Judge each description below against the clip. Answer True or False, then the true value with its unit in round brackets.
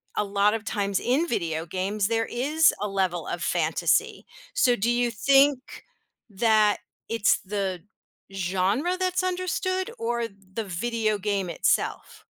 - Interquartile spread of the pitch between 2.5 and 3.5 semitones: False (4.5 semitones)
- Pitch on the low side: False (215 Hz)